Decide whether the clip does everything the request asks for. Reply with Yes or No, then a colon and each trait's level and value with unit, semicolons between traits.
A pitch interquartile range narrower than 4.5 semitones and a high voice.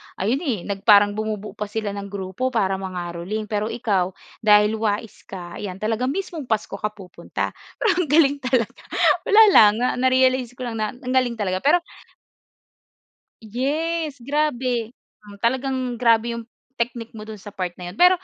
Yes: average, 4.0 semitones; high, 225 Hz